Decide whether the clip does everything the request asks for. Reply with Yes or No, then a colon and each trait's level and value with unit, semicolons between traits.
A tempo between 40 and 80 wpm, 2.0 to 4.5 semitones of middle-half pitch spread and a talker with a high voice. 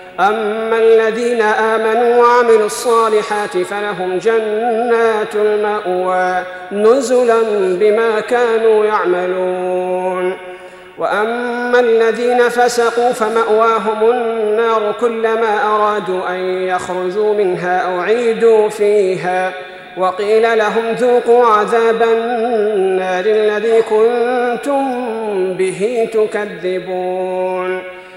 Yes: average, 70 wpm; average, 3.6 semitones; high, 215 Hz